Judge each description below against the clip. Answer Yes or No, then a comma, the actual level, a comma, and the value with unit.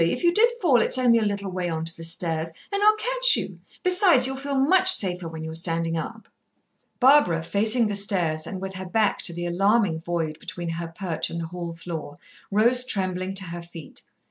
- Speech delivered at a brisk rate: Yes, fast, 210 wpm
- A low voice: No, medium, 185 Hz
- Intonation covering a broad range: Yes, wide, 6.7 semitones